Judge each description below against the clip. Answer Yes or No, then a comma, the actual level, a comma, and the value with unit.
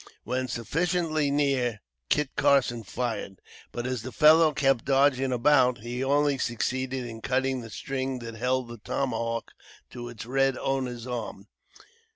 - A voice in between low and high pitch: No, low, 130 Hz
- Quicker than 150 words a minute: No, average, 145 wpm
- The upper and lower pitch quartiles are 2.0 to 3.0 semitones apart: Yes, narrow, 2.4 semitones